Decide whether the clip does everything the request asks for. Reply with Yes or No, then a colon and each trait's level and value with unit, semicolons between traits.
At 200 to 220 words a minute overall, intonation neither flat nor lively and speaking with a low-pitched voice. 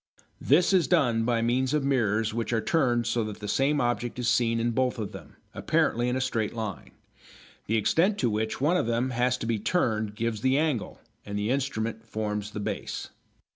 Yes: fast, 205 wpm; average, 3.0 semitones; low, 120 Hz